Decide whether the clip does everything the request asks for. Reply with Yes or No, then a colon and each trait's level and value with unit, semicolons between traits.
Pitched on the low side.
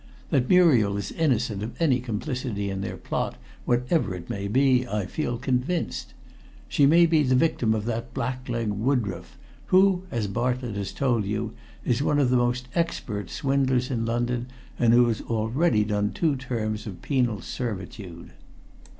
Yes: low, 120 Hz